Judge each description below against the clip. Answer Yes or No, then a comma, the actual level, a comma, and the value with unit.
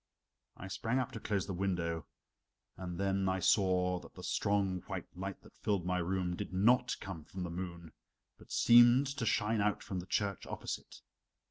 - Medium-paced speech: Yes, average, 185 wpm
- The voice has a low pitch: Yes, very low, 95 Hz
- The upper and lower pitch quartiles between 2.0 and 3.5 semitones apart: Yes, narrow, 2.4 semitones